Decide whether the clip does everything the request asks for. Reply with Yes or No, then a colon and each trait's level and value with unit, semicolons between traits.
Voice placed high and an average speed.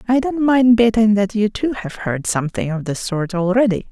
No: high, 215 Hz; fast, 215 wpm